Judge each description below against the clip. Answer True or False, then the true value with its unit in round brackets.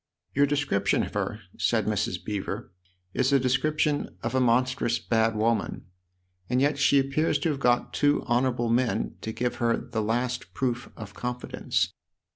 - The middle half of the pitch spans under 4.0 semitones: True (3.3 semitones)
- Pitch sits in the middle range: False (125 Hz)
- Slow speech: False (170 wpm)